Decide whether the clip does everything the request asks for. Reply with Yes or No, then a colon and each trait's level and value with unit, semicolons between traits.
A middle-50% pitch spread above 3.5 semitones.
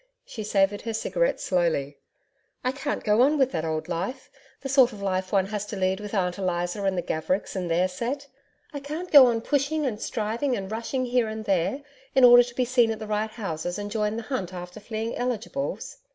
Yes: average, 5.1 semitones